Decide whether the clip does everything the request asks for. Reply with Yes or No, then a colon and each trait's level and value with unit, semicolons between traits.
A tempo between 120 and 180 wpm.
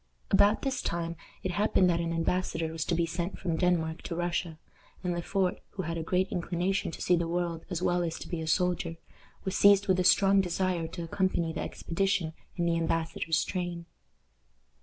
No: average, 200 wpm